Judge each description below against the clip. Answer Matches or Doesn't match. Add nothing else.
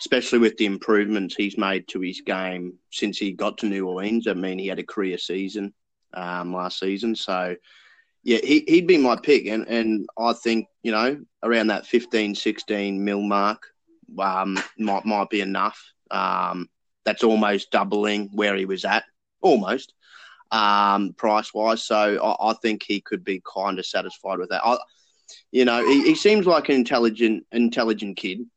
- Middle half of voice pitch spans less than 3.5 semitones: Matches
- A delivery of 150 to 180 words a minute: Matches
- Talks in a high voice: Doesn't match